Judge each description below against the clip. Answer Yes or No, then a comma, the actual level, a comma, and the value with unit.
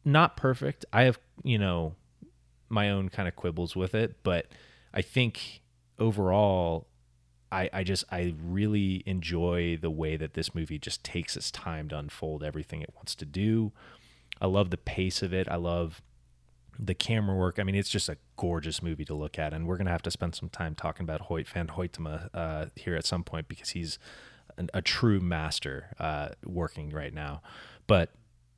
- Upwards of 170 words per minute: Yes, average, 190 wpm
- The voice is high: No, very low, 85 Hz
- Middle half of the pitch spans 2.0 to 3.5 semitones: No, average, 4.3 semitones